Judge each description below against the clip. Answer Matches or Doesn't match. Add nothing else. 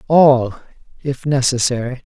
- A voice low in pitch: Matches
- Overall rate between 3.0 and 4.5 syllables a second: Matches